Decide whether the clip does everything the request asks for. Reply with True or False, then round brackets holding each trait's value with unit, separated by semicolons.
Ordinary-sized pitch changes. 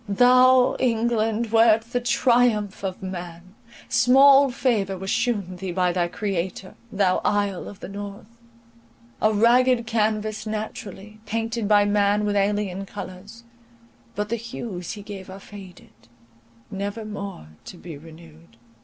True (3.1 semitones)